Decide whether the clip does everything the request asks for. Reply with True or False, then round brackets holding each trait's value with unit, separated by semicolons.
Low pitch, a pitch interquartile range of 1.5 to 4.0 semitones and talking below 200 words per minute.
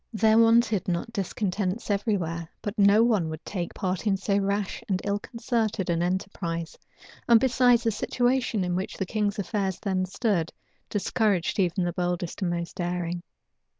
False (195 Hz; 3.7 semitones; 165 wpm)